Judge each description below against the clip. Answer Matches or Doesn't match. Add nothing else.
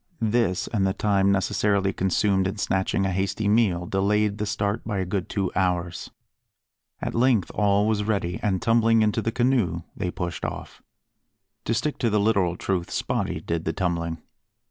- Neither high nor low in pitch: Doesn't match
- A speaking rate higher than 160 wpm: Matches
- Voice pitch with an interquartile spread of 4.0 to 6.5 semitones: Doesn't match